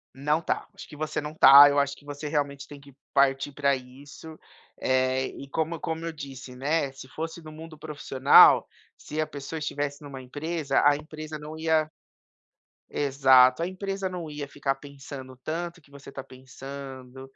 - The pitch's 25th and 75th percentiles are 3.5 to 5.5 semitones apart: No, narrow, 2.4 semitones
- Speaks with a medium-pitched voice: Yes, medium, 145 Hz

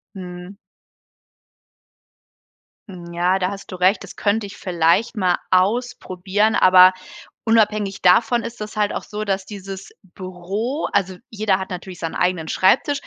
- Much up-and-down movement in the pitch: No, narrow, 2.6 semitones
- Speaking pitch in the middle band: No, high, 195 Hz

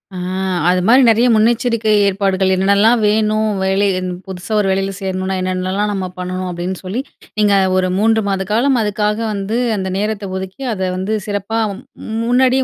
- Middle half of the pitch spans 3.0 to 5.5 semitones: No, narrow, 2.6 semitones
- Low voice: No, high, 200 Hz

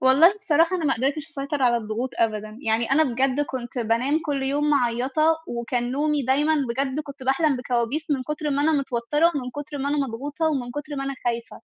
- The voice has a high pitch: Yes, very high, 275 Hz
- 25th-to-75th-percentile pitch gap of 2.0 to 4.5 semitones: Yes, average, 3.3 semitones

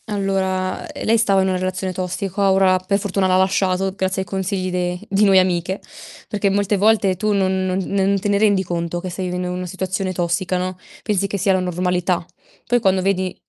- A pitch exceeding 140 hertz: Yes, high, 190 Hz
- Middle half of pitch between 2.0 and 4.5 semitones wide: No, narrow, 1.3 semitones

